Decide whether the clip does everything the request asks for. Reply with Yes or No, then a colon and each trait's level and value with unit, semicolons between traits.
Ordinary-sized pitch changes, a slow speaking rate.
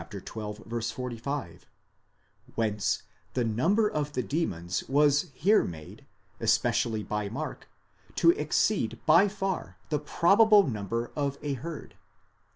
No: wide, 7.1 semitones; slow, 110 wpm